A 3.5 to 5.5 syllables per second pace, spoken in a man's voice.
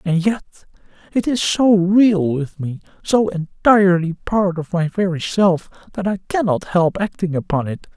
Yes: 4.2 syllables/s; male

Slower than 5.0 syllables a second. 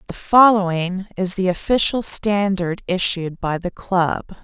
Yes: 4.0 syllables/s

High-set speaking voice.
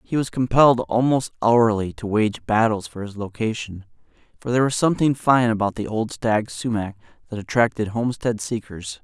No: low, 115 Hz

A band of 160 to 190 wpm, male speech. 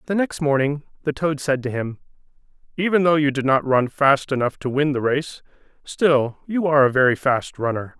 No: fast, 205 wpm; male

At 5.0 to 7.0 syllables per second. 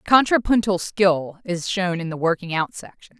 No: 4.6 syllables/s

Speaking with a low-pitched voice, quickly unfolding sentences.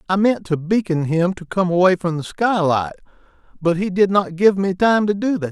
No: medium, 185 Hz; fast, 230 wpm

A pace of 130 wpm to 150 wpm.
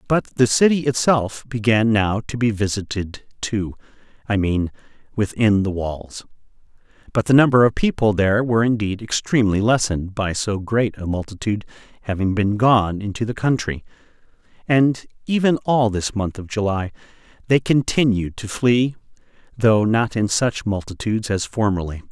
Yes: average, 145 wpm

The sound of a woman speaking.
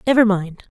Yes: female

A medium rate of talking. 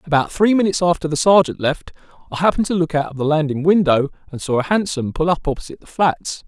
No: fast, 230 wpm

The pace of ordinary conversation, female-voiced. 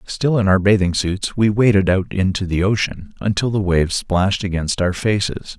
No: average, 195 wpm; male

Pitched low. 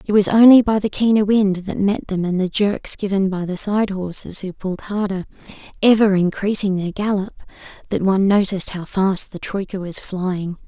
No: high, 195 Hz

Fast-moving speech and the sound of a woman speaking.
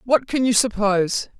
No: average, 170 wpm; female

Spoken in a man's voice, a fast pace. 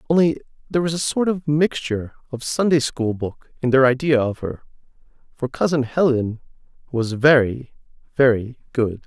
No: male; average, 150 wpm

